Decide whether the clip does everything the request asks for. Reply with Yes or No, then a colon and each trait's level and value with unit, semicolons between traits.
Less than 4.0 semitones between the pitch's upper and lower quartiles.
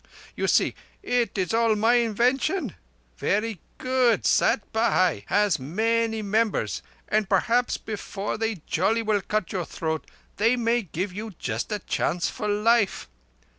Yes: average, 3.0 semitones